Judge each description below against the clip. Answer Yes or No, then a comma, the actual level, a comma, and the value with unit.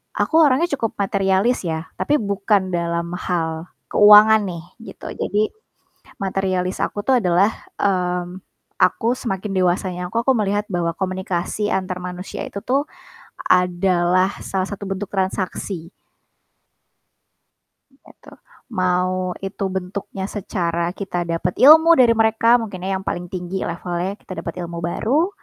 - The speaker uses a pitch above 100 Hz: Yes, high, 190 Hz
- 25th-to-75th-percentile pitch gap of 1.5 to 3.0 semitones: Yes, average, 2.7 semitones